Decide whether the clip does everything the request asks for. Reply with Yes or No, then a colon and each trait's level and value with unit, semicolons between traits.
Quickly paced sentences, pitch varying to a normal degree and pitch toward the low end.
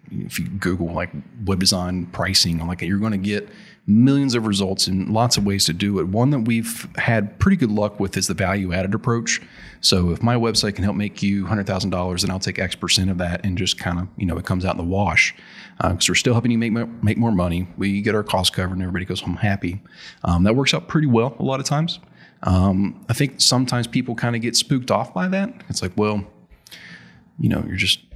Yes: fast, 240 wpm; average, 4.0 semitones; low, 100 Hz